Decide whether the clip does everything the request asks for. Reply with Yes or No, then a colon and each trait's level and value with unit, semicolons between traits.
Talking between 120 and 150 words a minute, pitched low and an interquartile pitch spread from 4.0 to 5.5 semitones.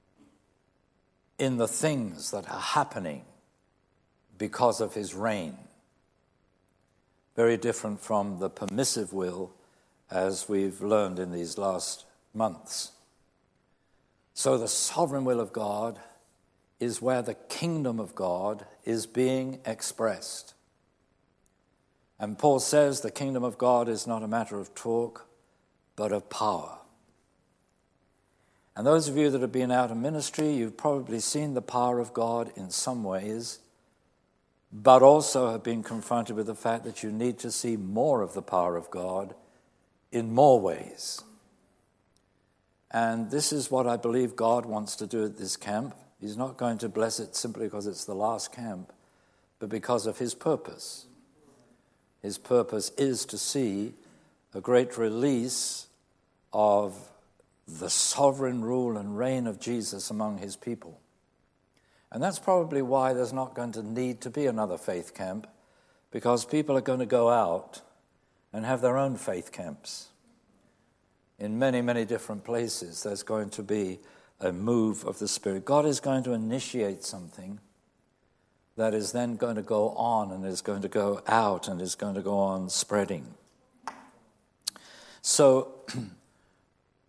No: average, 145 wpm; low, 115 Hz; average, 3.5 semitones